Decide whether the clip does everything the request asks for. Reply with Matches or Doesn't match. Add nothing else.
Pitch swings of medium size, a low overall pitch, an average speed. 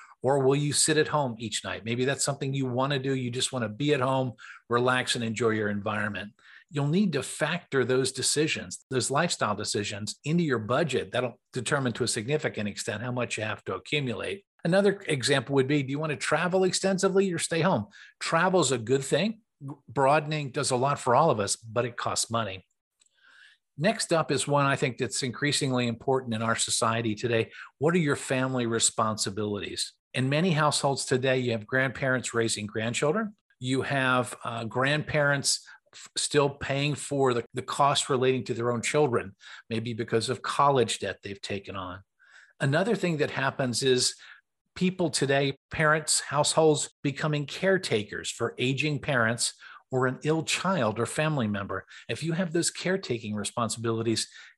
Matches